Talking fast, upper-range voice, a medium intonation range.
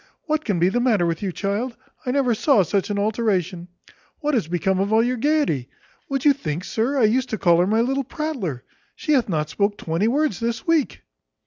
No: fast, 215 wpm; high, 220 Hz; wide, 6.3 semitones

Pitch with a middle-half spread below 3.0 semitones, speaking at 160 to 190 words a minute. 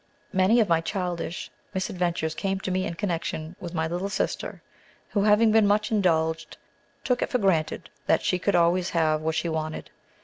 No: average, 3.4 semitones; average, 180 wpm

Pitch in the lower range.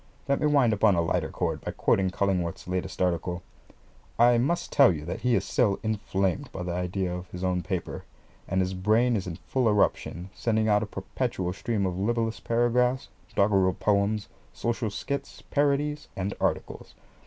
Yes: low, 100 Hz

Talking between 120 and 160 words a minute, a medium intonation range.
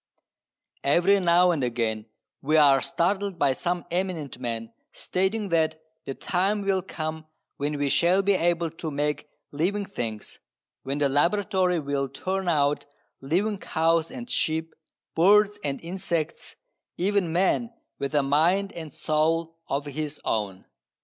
Yes: average, 140 wpm; average, 4.6 semitones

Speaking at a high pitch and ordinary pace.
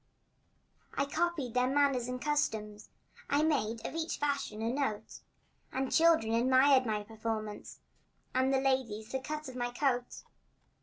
Yes: very high, 260 Hz; average, 150 wpm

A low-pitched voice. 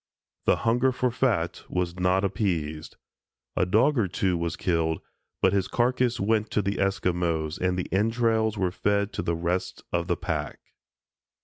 Yes: very low, 95 Hz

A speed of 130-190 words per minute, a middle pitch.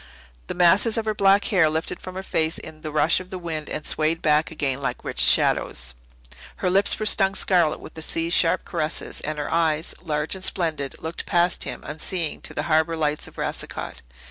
No: fast, 205 wpm; medium, 160 Hz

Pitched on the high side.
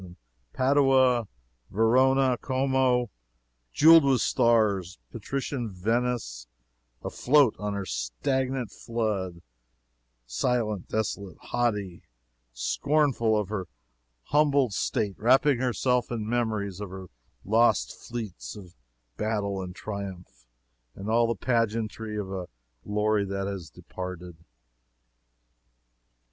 No: low, 110 Hz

